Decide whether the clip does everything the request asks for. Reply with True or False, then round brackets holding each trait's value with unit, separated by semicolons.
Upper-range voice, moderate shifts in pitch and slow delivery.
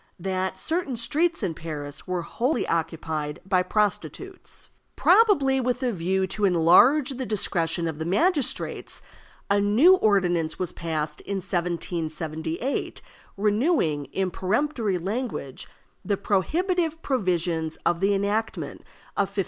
False (195 Hz; 7.0 semitones; 125 wpm)